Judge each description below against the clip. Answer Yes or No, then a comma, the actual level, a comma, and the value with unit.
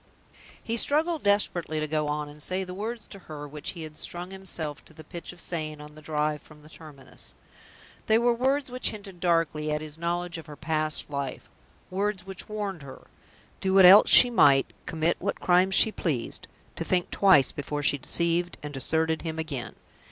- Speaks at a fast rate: No, average, 195 wpm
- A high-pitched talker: No, medium, 165 Hz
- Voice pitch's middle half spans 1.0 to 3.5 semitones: No, average, 4.1 semitones